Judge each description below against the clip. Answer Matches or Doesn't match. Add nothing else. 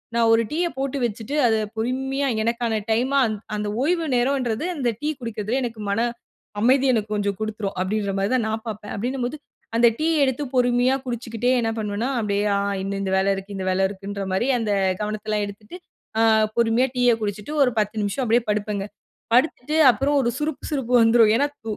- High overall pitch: Matches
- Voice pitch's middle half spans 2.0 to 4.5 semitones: Matches